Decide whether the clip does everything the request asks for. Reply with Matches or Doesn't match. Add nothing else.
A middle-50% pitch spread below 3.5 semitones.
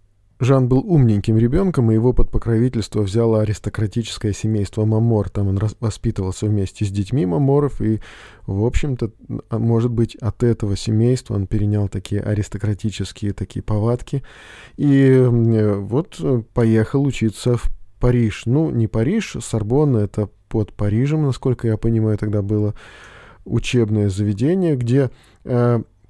Matches